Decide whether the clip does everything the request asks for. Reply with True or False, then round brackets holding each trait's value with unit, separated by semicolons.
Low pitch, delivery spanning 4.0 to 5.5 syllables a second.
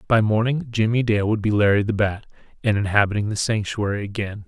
False (105 Hz; 5.9 syllables/s)